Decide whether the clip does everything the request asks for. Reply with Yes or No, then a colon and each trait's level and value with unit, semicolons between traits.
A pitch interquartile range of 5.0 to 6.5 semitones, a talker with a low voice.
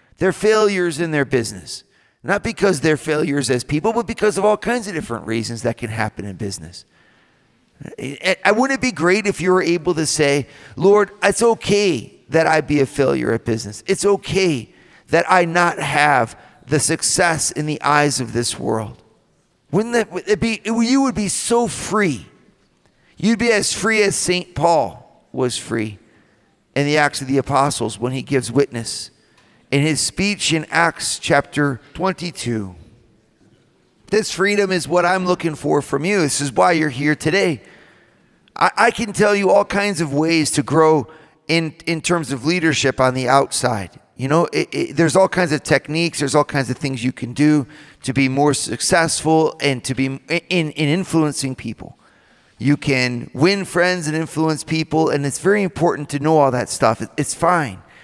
No: average, 5.3 semitones; medium, 155 Hz